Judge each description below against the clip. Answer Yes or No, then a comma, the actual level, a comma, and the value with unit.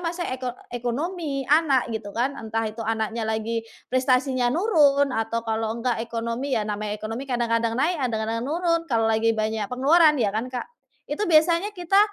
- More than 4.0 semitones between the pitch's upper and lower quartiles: Yes, average, 4.8 semitones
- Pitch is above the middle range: Yes, high, 245 Hz